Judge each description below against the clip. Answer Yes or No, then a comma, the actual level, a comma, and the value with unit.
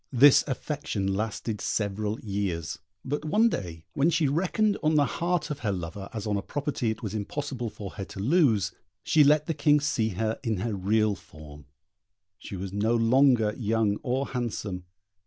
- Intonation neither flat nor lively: No, wide, 6.2 semitones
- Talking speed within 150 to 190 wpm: Yes, average, 175 wpm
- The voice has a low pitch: Yes, low, 110 Hz